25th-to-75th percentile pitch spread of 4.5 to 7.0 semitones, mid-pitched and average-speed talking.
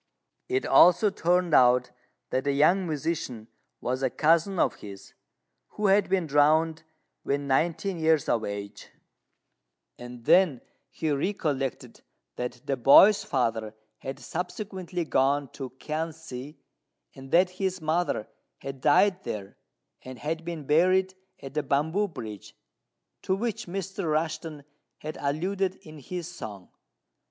No: average, 5.1 semitones; medium, 155 Hz; slow, 130 wpm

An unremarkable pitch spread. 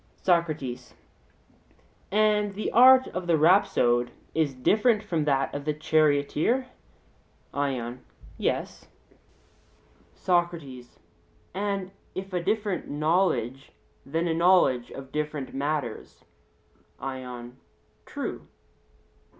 No: wide, 5.7 semitones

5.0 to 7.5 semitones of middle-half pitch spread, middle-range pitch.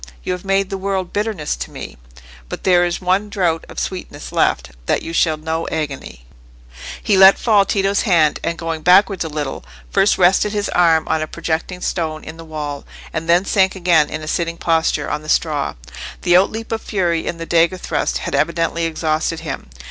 No: average, 3.2 semitones; medium, 170 Hz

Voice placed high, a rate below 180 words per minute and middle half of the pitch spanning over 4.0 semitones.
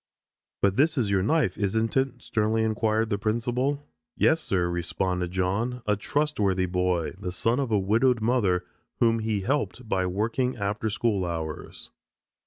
No: low, 110 Hz; average, 155 wpm; average, 4.4 semitones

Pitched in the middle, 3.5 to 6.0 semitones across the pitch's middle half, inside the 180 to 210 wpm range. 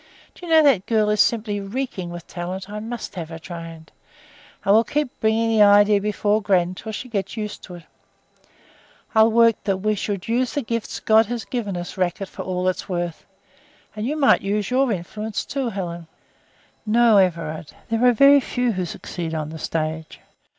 No: high, 210 Hz; average, 4.3 semitones; average, 190 wpm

